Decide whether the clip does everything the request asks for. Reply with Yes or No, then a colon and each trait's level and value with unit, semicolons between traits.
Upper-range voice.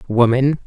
No: low, 135 Hz